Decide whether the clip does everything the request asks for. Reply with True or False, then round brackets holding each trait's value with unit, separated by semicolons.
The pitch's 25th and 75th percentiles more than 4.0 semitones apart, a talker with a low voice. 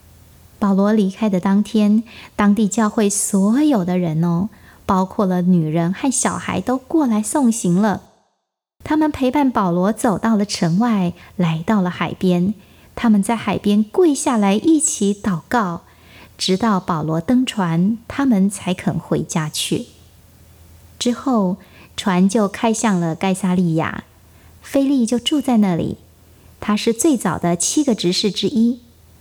False (4.7 semitones; 200 Hz)